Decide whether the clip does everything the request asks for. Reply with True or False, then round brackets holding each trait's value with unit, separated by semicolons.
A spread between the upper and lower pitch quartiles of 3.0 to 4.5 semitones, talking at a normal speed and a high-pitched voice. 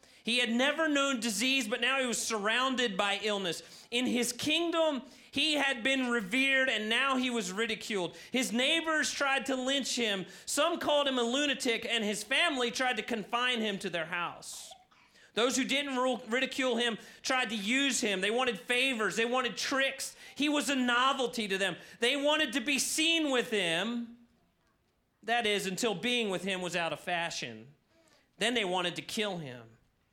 True (4.1 semitones; 175 wpm; 245 Hz)